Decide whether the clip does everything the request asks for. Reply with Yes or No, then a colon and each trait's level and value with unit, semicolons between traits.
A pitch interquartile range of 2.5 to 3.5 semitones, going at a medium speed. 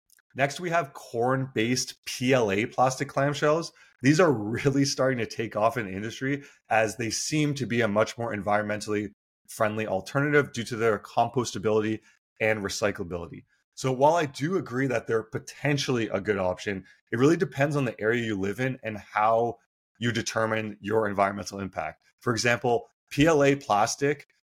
No: average, 4.2 semitones; average, 160 wpm